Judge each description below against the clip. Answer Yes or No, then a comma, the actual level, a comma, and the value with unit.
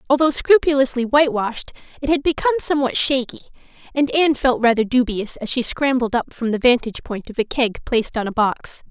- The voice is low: No, very high, 255 Hz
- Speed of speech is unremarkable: Yes, average, 190 wpm